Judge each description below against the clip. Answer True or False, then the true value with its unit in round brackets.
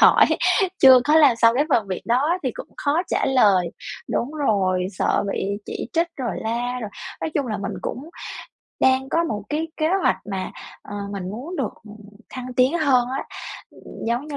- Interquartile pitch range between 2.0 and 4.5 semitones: False (5.2 semitones)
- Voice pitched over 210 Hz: True (255 Hz)